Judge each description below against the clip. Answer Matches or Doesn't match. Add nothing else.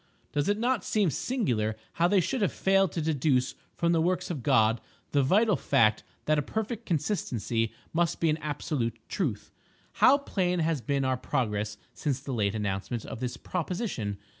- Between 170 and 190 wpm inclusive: Matches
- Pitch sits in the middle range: Matches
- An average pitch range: Doesn't match